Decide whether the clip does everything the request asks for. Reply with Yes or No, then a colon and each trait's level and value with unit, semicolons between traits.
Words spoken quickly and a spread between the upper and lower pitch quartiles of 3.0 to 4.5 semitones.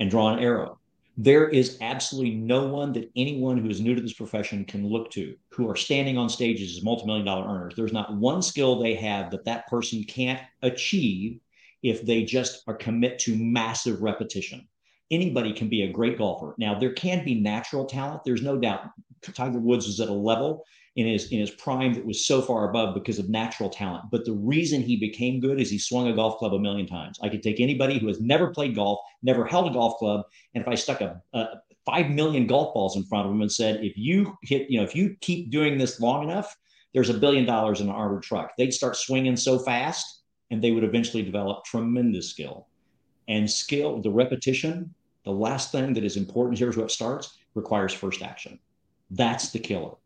Yes: fast, 215 wpm; average, 3.4 semitones